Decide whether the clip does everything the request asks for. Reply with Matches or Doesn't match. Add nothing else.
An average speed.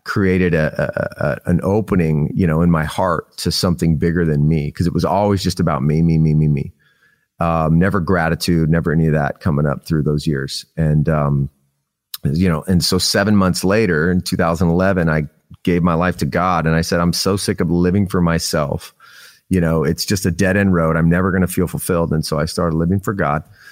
Doesn't match